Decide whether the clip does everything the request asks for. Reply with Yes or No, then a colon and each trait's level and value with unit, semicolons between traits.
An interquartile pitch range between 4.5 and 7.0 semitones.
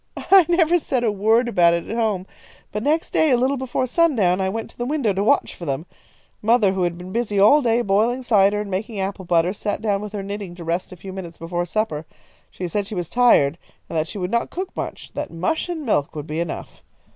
Yes: average, 5.1 semitones